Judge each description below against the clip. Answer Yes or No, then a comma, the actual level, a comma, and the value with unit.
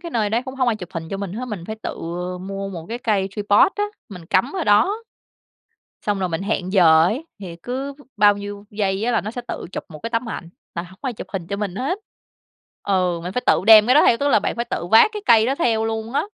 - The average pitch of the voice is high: Yes, high, 210 Hz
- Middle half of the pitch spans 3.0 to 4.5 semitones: Yes, average, 4.2 semitones